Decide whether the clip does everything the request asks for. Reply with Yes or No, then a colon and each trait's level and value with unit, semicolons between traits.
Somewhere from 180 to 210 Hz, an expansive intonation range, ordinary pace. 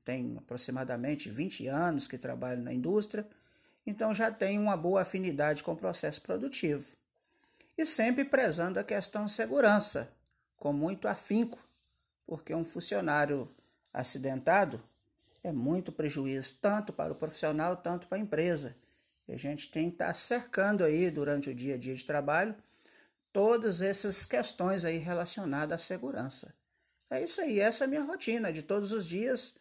Yes: medium, 185 Hz; wide, 6.7 semitones; average, 155 wpm